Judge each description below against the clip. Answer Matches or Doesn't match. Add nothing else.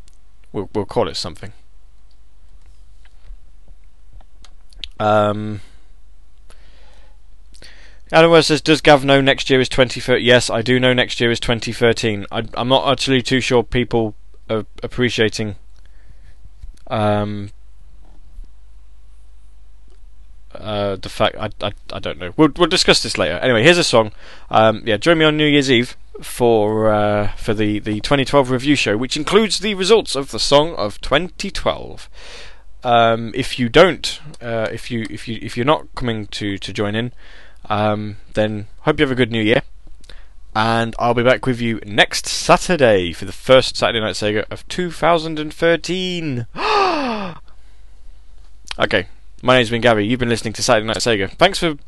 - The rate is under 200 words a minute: Matches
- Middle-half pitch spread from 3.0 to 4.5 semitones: Doesn't match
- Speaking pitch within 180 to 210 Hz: Doesn't match